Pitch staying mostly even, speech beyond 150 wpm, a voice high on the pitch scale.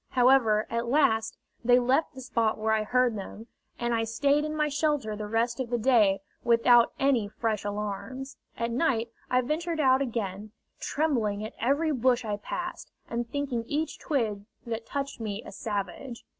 No: average, 3.6 semitones; average, 170 wpm; high, 235 Hz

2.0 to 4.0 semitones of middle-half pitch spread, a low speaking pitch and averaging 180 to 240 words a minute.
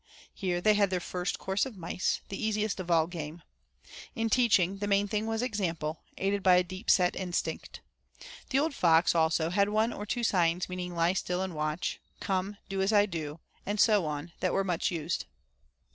No: average, 3.3 semitones; medium, 185 Hz; average, 195 wpm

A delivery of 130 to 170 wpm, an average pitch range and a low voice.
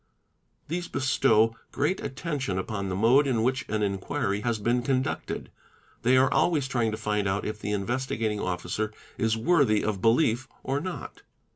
Yes: average, 160 wpm; average, 4.1 semitones; low, 115 Hz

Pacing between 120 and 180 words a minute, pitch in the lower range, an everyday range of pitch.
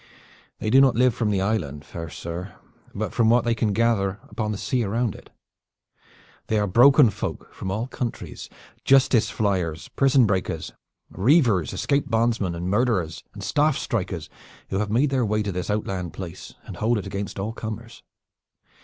Yes: average, 170 wpm; low, 105 Hz; average, 3.9 semitones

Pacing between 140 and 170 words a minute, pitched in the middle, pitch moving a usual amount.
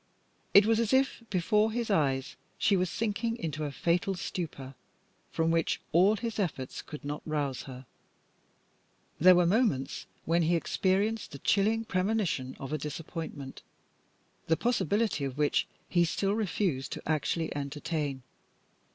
No: average, 145 wpm; medium, 170 Hz; wide, 6.0 semitones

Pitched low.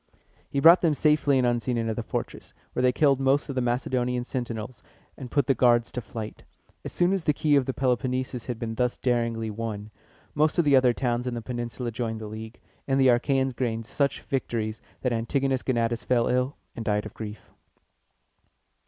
Yes: low, 125 Hz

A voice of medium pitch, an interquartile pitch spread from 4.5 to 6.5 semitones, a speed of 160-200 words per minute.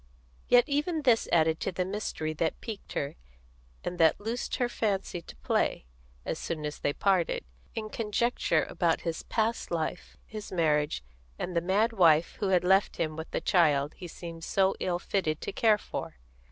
Yes: medium, 180 Hz; average, 4.8 semitones; average, 180 wpm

